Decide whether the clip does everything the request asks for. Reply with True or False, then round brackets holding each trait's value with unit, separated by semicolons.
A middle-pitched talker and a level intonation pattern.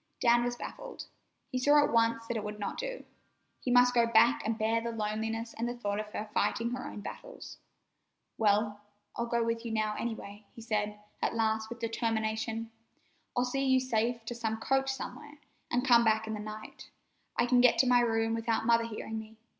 False (230 Hz; 1.8 semitones)